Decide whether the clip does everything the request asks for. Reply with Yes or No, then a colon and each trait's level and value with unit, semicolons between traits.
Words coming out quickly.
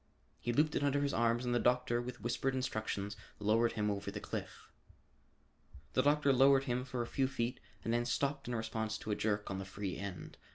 Yes: fast, 210 wpm